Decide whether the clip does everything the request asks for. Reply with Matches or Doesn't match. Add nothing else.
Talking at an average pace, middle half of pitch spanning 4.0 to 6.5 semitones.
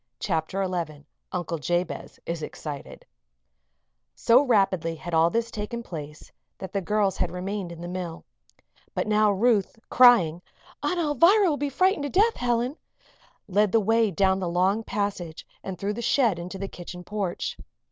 Matches